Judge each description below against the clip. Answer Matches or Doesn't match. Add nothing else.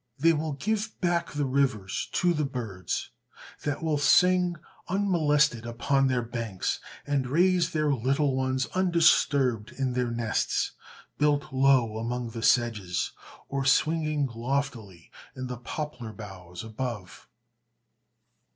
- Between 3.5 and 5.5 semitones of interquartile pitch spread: Matches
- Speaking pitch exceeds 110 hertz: Matches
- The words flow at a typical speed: Doesn't match